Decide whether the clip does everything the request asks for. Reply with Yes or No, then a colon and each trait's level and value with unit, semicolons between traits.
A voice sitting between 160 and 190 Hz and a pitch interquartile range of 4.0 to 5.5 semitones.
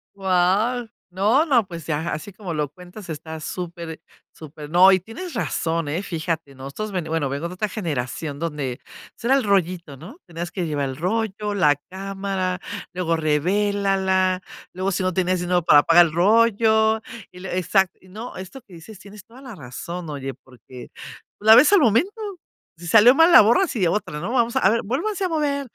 Yes: medium, 185 Hz; average, 4.9 semitones